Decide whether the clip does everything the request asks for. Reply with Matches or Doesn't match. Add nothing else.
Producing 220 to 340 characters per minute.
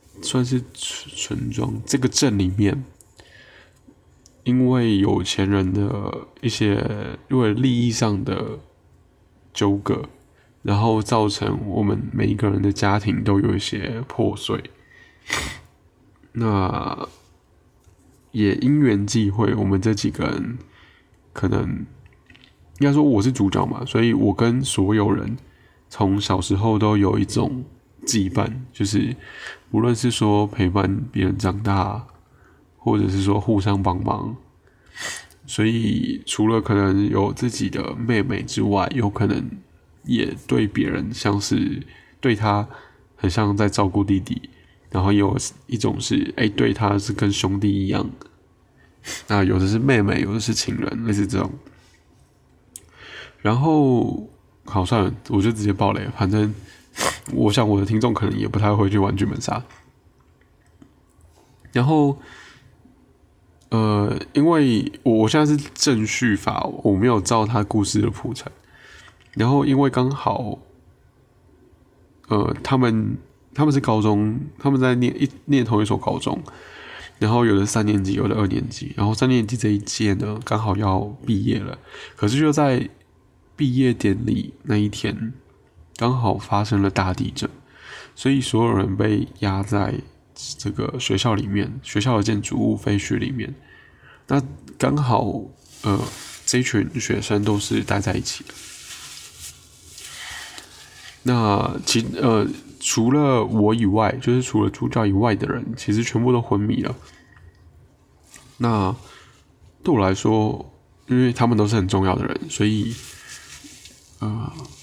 Doesn't match